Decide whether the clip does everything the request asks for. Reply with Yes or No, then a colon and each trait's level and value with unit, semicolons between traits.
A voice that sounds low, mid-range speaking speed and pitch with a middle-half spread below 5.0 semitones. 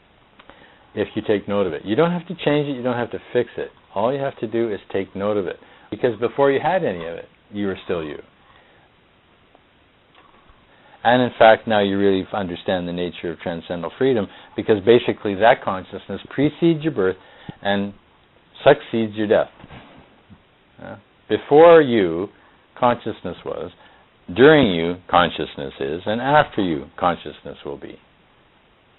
No: low, 110 Hz; average, 155 wpm; wide, 5.4 semitones